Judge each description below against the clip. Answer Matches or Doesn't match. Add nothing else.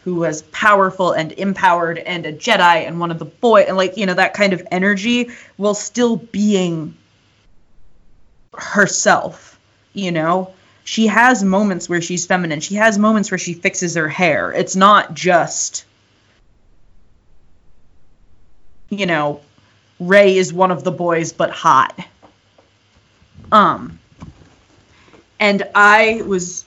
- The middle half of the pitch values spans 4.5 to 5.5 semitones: Matches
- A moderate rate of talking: Doesn't match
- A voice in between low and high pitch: Matches